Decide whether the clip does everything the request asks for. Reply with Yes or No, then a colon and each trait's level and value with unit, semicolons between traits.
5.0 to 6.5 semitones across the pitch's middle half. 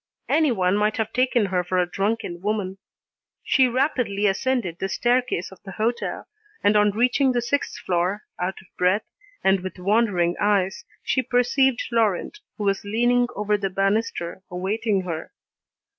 No: average, 4.2 semitones